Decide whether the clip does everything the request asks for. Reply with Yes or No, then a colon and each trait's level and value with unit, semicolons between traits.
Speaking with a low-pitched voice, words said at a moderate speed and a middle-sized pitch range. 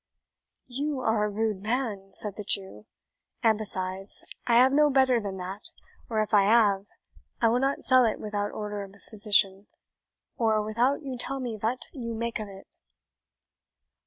No: high, 215 Hz; average, 170 wpm; average, 3.3 semitones